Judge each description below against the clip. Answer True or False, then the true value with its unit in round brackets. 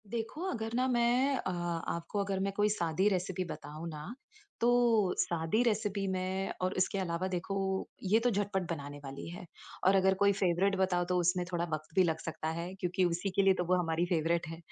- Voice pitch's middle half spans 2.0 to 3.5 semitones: True (2.9 semitones)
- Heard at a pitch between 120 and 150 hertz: False (185 Hz)